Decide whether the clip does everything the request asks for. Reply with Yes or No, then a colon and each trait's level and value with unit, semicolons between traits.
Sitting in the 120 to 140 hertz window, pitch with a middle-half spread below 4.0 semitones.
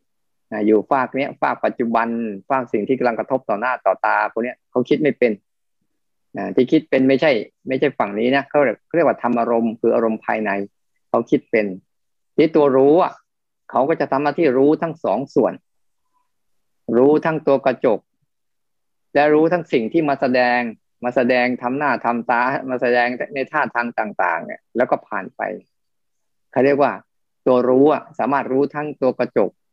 Yes: low, 130 Hz; average, 3.5 semitones